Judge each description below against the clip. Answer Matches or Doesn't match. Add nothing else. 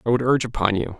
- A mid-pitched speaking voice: Doesn't match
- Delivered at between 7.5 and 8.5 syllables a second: Matches